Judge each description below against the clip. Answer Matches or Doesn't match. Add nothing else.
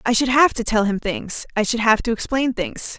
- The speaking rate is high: Matches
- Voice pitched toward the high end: Matches